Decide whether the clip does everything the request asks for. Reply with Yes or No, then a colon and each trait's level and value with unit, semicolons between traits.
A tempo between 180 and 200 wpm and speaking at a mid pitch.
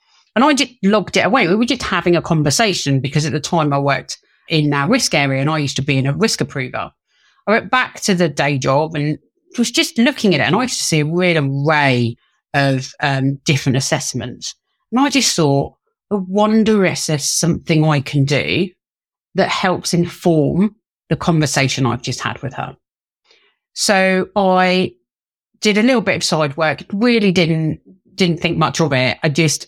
Yes: average, 195 wpm; medium, 160 Hz